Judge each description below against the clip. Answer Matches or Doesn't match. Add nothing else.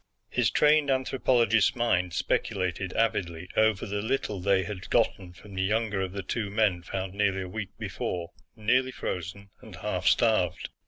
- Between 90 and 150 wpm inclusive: Doesn't match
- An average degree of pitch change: Matches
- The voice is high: Doesn't match